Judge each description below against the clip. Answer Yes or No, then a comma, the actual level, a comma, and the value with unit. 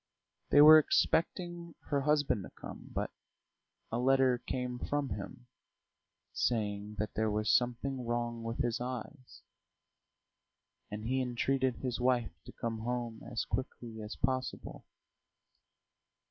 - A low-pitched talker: Yes, low, 125 Hz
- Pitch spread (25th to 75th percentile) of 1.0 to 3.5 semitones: Yes, narrow, 2.6 semitones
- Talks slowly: Yes, slow, 125 wpm